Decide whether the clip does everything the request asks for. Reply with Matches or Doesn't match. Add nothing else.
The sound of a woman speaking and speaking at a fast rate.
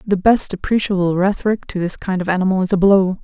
Matches